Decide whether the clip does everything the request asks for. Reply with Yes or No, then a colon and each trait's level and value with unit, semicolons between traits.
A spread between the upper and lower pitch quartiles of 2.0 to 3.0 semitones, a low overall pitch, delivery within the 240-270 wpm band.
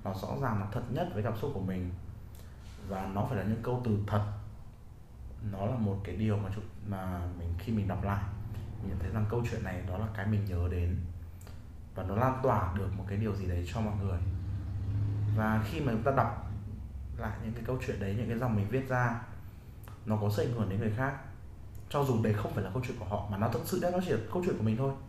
Yes: narrow, 2.4 semitones; low, 105 Hz; fast, 250 wpm